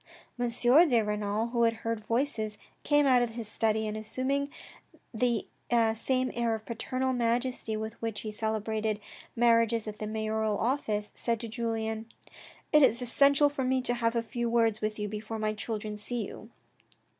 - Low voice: No, high, 230 Hz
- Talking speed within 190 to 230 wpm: No, average, 175 wpm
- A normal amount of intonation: No, narrow, 2.0 semitones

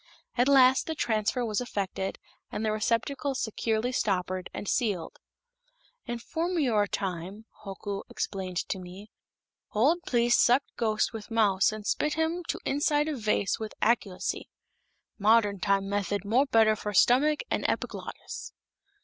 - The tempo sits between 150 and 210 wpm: No, average, 140 wpm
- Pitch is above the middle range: Yes, high, 220 Hz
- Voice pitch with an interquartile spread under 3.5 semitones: No, average, 4.0 semitones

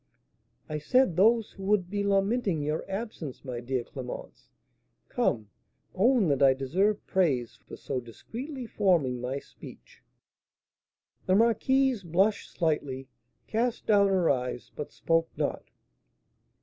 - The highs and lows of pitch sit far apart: Yes, wide, 7.9 semitones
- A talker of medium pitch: Yes, medium, 180 Hz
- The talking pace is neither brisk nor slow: No, slow, 125 wpm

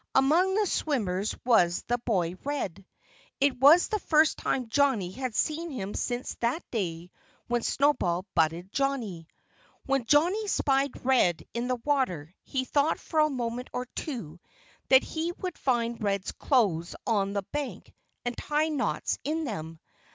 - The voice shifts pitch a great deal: Yes, wide, 6.7 semitones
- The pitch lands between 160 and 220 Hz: No, very high, 250 Hz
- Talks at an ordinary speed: Yes, average, 150 wpm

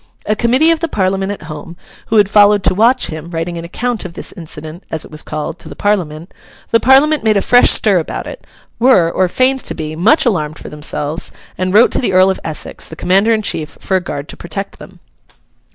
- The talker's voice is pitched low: No, medium, 185 Hz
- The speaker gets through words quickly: Yes, fast, 230 wpm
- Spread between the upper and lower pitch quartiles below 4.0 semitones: No, average, 5.3 semitones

